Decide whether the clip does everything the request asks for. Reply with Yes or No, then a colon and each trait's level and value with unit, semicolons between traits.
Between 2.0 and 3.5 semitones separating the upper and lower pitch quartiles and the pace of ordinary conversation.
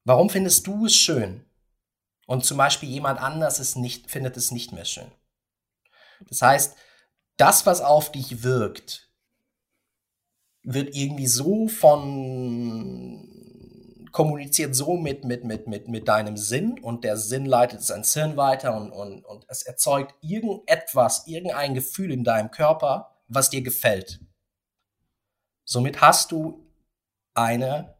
No: average, 4.1 semitones; average, 135 wpm